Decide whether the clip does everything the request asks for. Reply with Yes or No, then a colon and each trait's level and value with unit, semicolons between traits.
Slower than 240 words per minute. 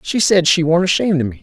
No: fast, 295 wpm